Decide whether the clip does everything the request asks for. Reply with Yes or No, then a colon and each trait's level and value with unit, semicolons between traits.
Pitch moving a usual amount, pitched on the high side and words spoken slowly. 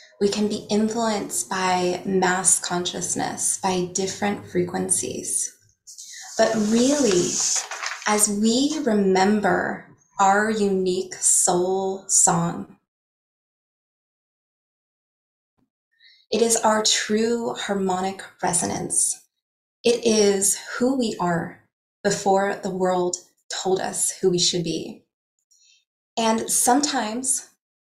Yes: average, 3.1 semitones; high, 200 Hz; slow, 90 wpm